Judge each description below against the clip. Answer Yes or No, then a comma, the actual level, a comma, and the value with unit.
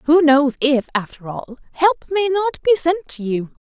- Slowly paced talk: No, average, 200 wpm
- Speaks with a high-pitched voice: Yes, very high, 295 Hz